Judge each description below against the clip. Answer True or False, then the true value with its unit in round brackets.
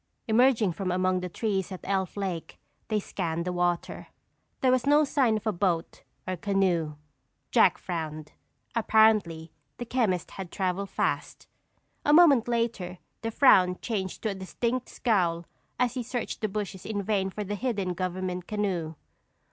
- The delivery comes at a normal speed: True (155 wpm)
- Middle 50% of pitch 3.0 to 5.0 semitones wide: True (3.9 semitones)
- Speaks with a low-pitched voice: False (195 Hz)